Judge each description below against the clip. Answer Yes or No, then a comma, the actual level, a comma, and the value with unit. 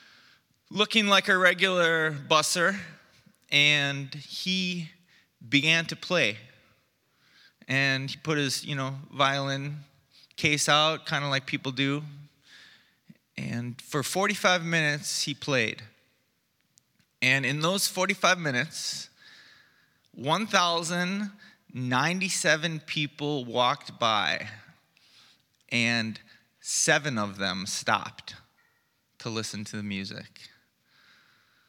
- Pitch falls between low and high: Yes, medium, 145 Hz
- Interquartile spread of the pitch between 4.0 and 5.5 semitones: Yes, average, 4.7 semitones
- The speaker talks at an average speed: No, slow, 95 wpm